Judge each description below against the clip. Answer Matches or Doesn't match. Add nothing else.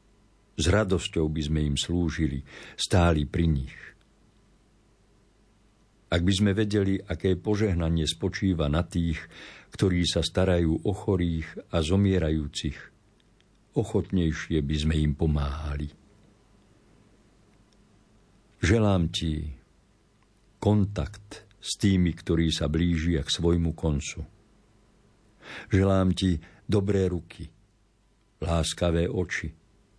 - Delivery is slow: Matches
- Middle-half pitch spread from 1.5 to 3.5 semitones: Doesn't match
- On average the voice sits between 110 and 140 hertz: Doesn't match